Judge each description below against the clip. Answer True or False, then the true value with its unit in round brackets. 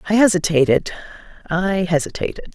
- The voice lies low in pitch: False (175 Hz)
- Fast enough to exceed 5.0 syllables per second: True (5.7 syllables/s)